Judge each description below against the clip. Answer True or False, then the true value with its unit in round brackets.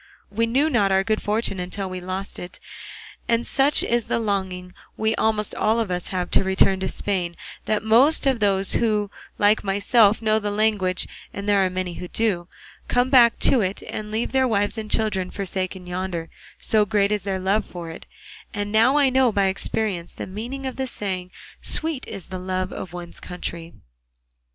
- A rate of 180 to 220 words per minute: True (190 wpm)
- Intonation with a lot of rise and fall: False (3.1 semitones)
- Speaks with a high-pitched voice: True (205 Hz)